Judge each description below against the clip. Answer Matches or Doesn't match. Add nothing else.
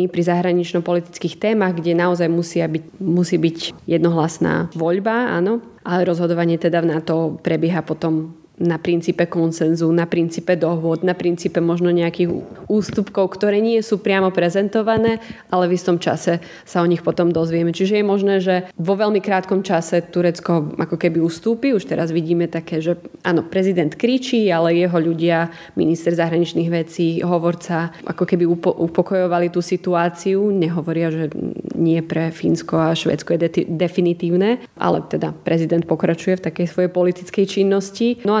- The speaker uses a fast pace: Doesn't match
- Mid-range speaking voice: Matches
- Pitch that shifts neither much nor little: Doesn't match